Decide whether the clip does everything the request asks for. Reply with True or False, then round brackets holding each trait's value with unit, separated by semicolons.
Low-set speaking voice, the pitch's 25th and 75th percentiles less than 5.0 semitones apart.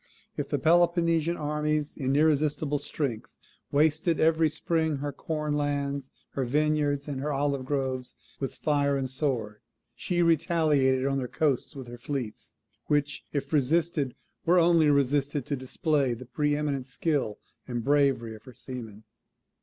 False (145 Hz; 2.6 semitones)